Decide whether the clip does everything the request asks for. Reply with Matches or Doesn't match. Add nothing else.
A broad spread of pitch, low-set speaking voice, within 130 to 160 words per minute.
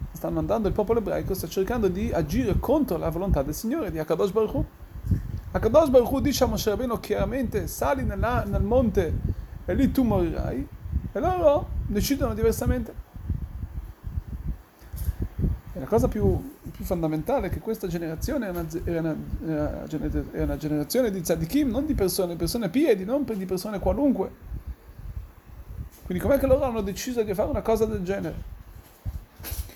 Doesn't match